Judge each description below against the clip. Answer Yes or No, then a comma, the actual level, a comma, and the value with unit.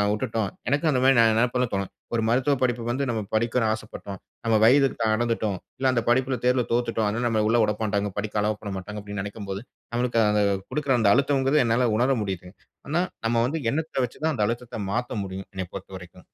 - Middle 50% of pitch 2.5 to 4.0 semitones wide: Yes, average, 3.5 semitones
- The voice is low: Yes, low, 115 Hz